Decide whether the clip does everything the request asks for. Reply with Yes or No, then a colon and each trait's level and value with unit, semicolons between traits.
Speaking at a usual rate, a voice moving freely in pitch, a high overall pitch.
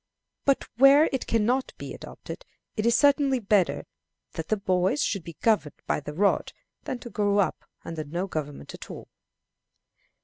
Yes: average, 170 wpm; wide, 6.6 semitones; high, 210 Hz